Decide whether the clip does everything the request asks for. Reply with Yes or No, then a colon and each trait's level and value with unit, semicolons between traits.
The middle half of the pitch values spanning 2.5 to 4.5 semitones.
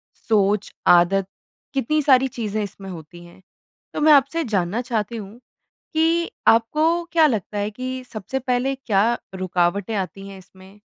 No: wide, 5.5 semitones